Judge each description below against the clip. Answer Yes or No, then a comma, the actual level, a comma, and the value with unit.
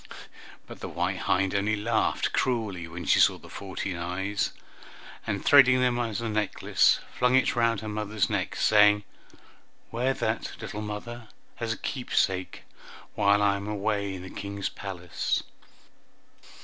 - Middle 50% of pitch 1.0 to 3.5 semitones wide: Yes, average, 2.9 semitones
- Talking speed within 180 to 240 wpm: No, average, 150 wpm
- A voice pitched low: Yes, low, 105 Hz